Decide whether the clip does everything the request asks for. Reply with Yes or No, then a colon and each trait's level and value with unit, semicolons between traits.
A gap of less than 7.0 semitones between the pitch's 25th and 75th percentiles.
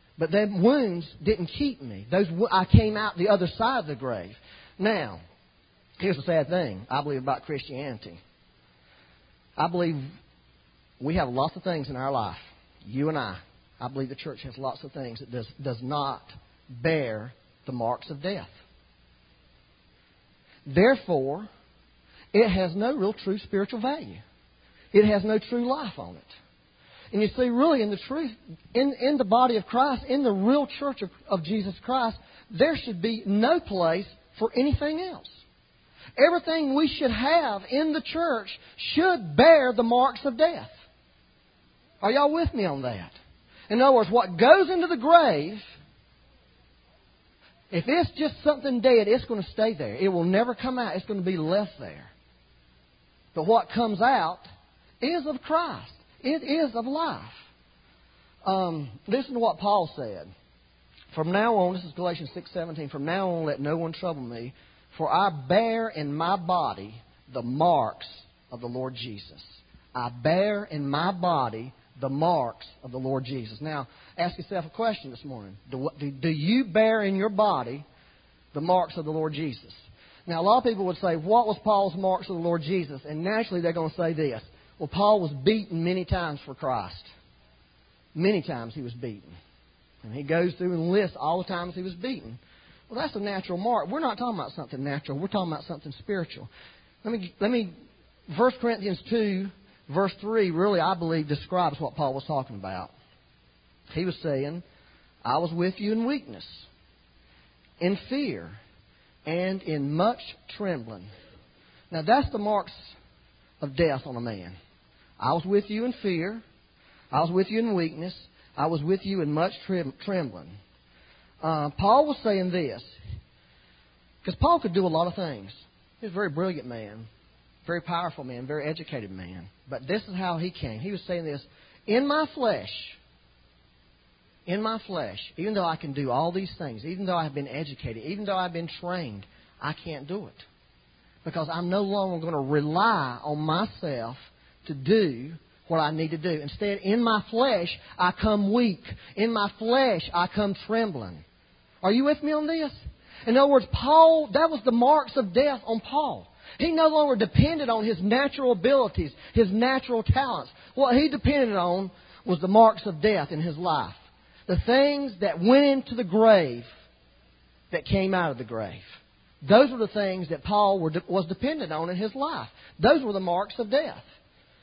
No: wide, 8.7 semitones